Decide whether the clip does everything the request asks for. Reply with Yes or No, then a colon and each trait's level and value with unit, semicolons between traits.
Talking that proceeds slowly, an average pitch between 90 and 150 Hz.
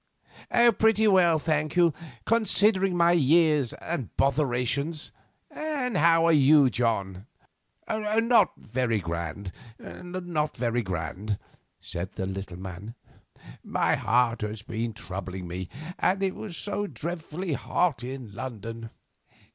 Yes: slow, 115 wpm; low, 135 Hz